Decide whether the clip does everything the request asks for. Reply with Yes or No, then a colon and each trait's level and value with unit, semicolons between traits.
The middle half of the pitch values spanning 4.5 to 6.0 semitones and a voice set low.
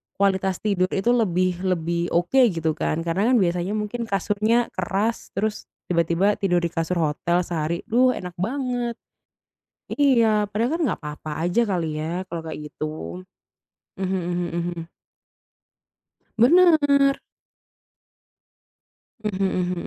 No: average, 4.8 semitones; medium, 185 Hz